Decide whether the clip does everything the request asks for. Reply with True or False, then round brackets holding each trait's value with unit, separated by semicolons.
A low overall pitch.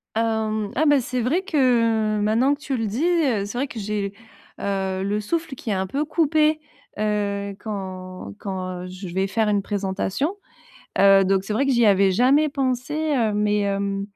False (210 Hz)